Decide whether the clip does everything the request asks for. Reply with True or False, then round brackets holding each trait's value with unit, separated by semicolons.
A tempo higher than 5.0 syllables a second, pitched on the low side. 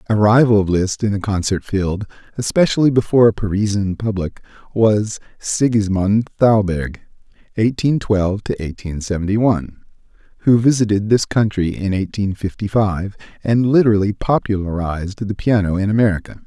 False (4.5 syllables/s; 105 Hz)